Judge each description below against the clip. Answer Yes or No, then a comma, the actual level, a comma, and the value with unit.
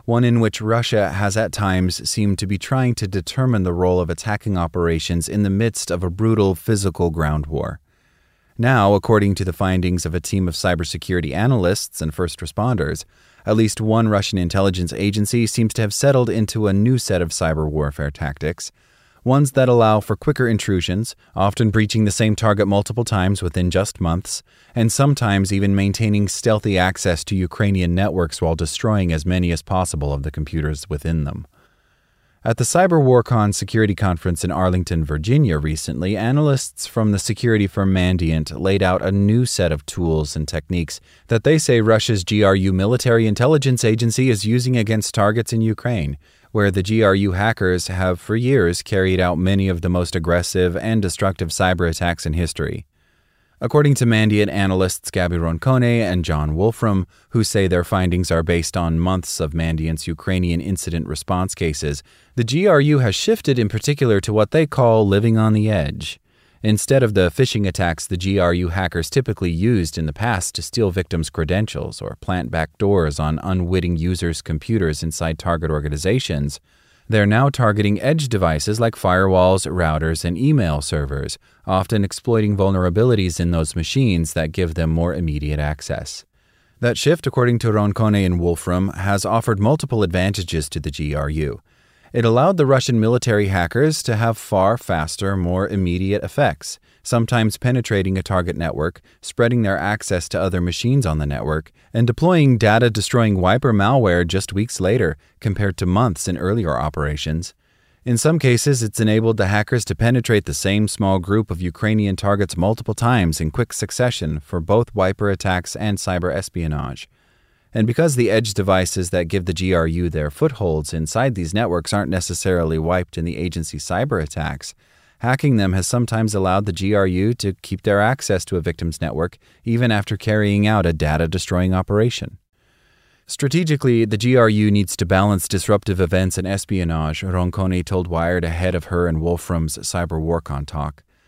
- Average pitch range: Yes, average, 4.4 semitones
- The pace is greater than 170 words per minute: No, average, 165 wpm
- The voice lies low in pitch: Yes, very low, 95 Hz